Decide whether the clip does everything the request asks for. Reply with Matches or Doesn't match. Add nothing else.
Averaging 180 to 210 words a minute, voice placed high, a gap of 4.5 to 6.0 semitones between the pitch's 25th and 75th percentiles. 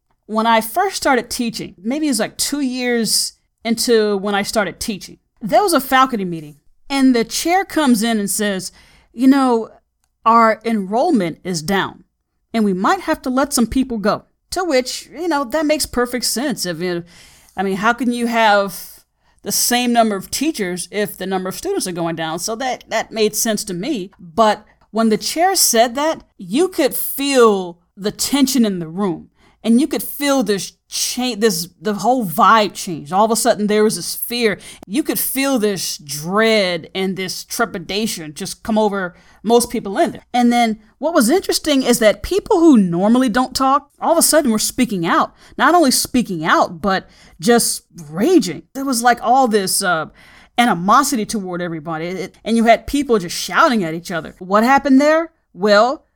Matches